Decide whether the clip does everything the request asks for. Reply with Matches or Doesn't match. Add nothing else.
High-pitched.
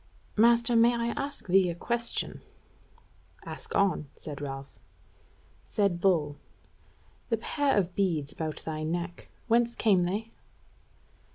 Matches